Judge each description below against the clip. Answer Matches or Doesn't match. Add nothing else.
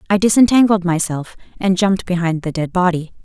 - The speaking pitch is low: Doesn't match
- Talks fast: Doesn't match